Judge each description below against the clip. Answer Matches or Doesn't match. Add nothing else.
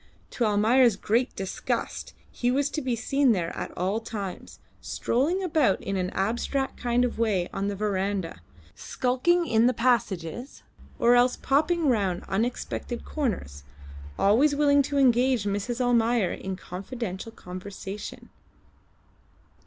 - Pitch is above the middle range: Matches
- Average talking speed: Doesn't match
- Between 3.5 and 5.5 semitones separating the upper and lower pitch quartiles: Matches